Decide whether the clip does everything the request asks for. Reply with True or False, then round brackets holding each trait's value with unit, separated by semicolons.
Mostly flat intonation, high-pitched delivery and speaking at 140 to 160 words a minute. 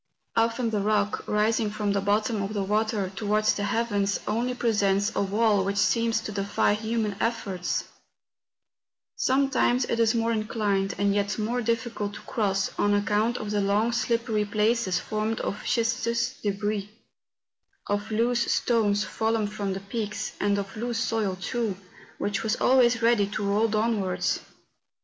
True (2.1 semitones; 215 Hz; 155 wpm)